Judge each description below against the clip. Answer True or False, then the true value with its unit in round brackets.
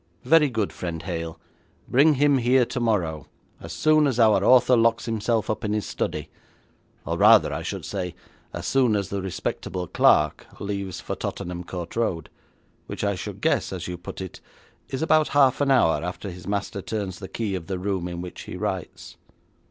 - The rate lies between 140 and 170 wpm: False (185 wpm)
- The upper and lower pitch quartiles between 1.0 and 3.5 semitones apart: False (5.4 semitones)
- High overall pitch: False (100 Hz)